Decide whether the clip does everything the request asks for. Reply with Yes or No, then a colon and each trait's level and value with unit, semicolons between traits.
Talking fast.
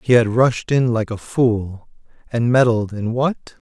No: average, 175 wpm